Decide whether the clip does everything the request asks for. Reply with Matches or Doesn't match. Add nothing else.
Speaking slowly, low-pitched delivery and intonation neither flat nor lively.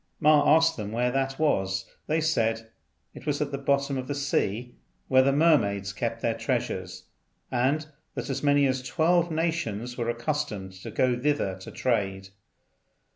Doesn't match